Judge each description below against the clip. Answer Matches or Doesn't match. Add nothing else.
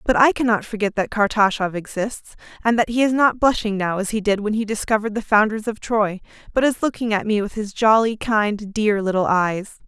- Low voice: Doesn't match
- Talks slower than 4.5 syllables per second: Doesn't match